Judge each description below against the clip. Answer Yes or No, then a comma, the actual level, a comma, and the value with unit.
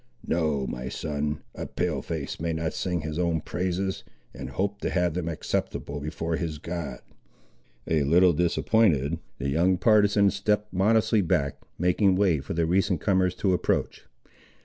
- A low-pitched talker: Yes, very low, 85 Hz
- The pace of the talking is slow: No, average, 155 wpm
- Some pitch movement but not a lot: Yes, average, 3.4 semitones